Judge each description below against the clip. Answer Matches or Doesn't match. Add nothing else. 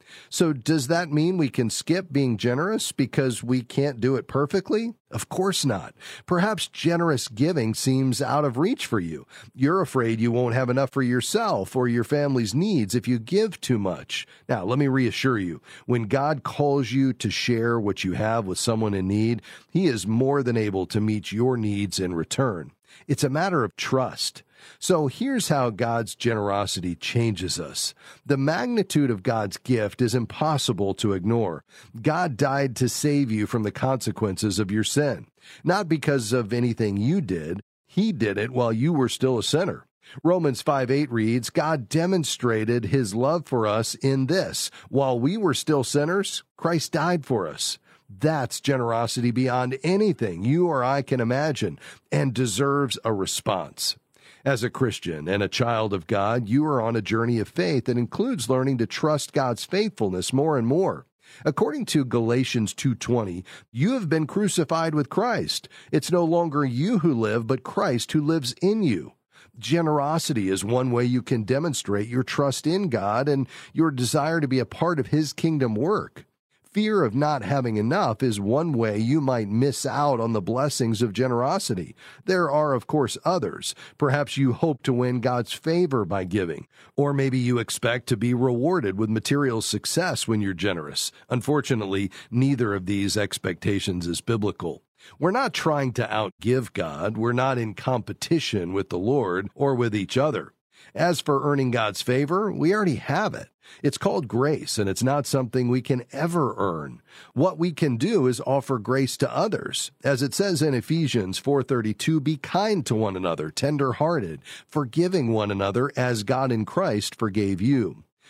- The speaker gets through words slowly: Doesn't match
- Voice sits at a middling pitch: Doesn't match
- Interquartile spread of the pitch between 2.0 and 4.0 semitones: Doesn't match